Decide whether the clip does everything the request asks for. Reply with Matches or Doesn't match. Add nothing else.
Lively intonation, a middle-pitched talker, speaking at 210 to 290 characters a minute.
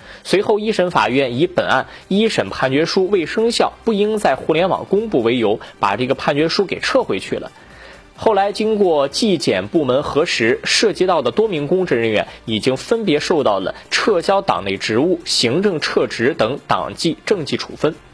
Matches